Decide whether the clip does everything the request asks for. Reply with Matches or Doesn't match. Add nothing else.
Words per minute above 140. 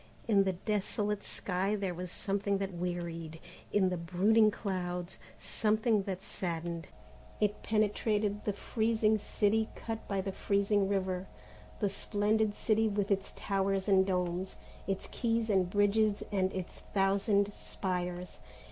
Doesn't match